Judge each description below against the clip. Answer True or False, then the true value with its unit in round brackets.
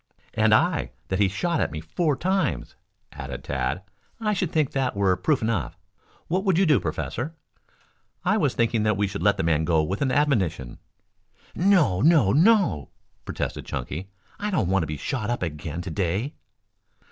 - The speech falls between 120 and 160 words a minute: False (180 wpm)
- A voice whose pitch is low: True (105 Hz)